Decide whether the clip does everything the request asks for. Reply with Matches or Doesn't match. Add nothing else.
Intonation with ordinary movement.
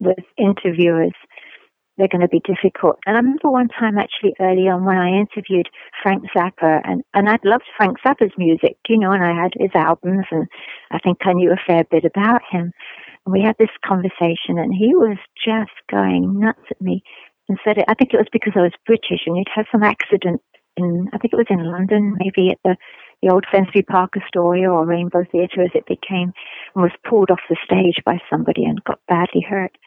Matches